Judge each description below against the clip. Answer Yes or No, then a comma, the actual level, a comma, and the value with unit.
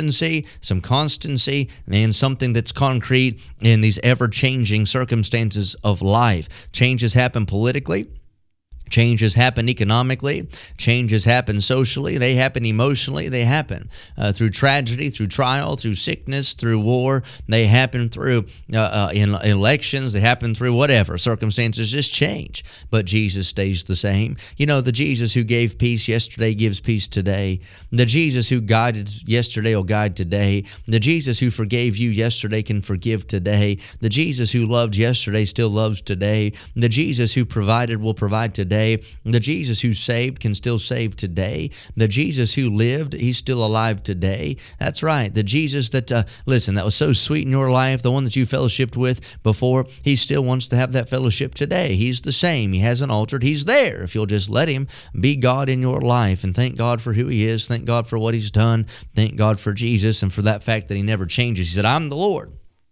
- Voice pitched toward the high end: No, low, 115 Hz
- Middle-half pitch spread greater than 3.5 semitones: No, average, 3.2 semitones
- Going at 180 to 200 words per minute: Yes, average, 185 wpm